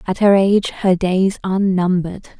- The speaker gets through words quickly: No, average, 175 wpm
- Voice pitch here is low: No, high, 190 Hz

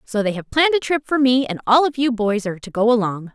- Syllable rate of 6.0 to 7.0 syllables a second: Yes, 6.3 syllables/s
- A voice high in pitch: Yes, high, 235 Hz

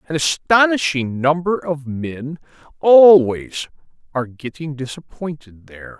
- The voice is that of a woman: No, male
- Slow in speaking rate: Yes, slow, 100 wpm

